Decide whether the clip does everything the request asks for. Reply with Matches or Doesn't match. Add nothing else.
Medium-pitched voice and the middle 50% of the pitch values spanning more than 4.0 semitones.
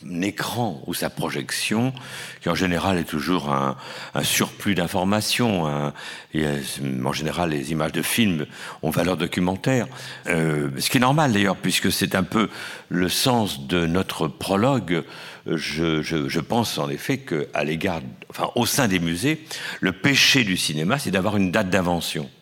Doesn't match